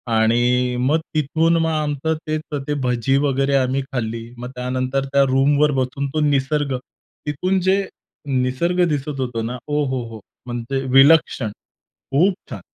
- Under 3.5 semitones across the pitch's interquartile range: Yes, average, 3.0 semitones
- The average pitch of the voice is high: No, low, 135 Hz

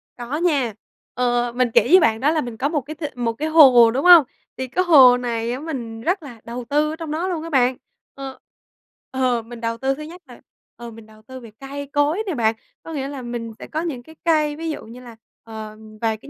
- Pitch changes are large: No, average, 4.5 semitones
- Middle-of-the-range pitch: No, very high, 260 Hz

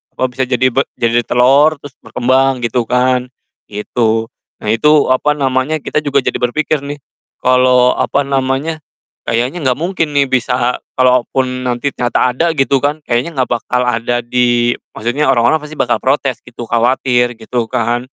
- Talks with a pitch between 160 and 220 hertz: No, low, 125 Hz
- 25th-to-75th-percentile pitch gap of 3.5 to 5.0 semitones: No, narrow, 2.4 semitones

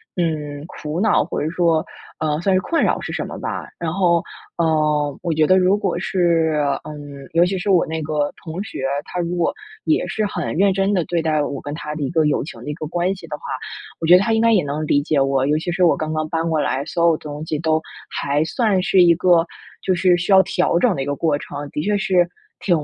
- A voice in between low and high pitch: Yes, medium, 165 Hz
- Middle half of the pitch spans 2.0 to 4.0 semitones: Yes, average, 3.2 semitones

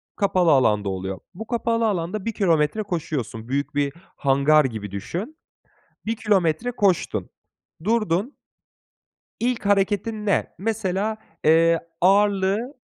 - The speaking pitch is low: No, high, 190 Hz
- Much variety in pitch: Yes, wide, 6.2 semitones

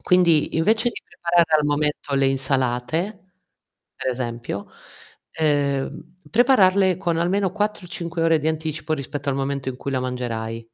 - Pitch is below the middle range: No, medium, 155 Hz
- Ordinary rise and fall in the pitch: Yes, average, 4.9 semitones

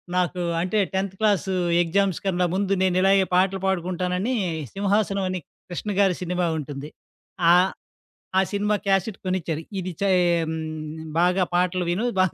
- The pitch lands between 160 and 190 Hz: Yes, medium, 185 Hz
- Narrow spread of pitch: Yes, narrow, 1.7 semitones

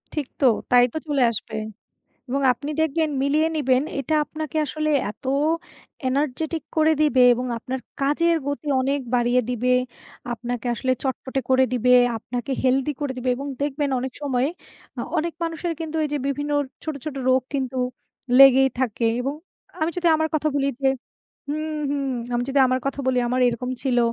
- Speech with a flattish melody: No, average, 3.1 semitones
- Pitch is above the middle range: Yes, very high, 275 Hz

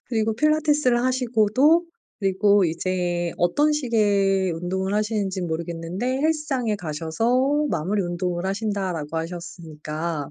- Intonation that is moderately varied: No, wide, 5.9 semitones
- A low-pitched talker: No, high, 195 Hz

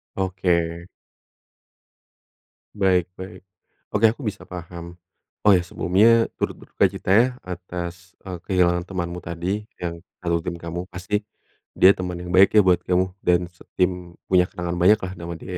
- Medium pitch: No, very low, 90 Hz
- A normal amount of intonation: No, narrow, 1.4 semitones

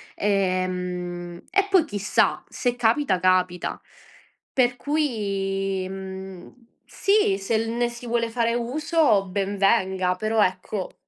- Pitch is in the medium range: No, high, 200 Hz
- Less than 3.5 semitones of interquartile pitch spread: No, average, 4.3 semitones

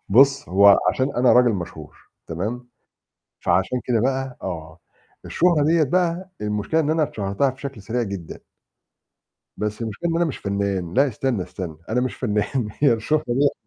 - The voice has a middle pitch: No, low, 120 Hz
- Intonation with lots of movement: Yes, wide, 5.8 semitones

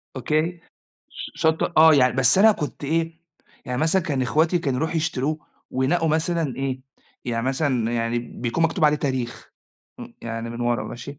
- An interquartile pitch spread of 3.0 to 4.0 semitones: No, average, 4.5 semitones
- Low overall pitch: No, medium, 145 Hz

